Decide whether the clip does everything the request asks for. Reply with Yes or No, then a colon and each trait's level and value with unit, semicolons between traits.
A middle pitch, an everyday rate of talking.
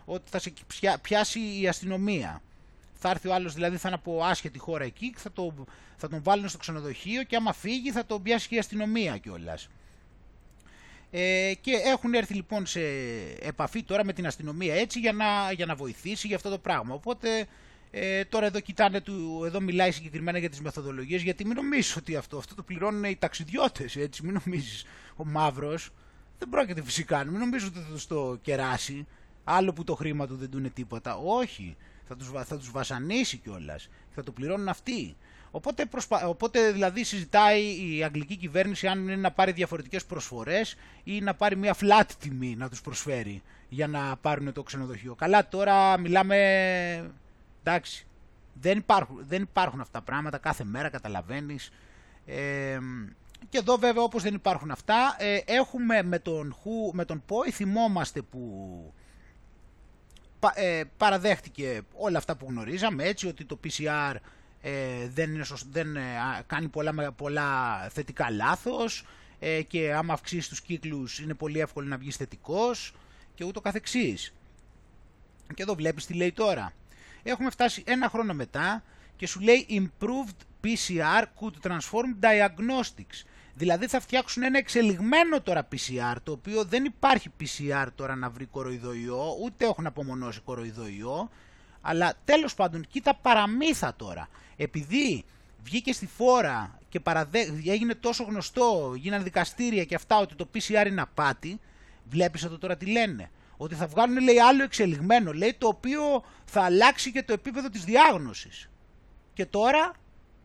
Yes: medium, 180 Hz; average, 160 wpm